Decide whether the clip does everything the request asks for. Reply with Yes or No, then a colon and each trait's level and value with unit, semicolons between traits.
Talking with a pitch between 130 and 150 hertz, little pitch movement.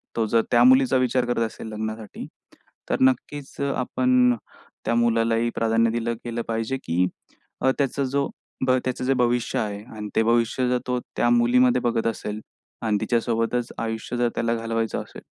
No: low, 120 Hz; narrow, 1.9 semitones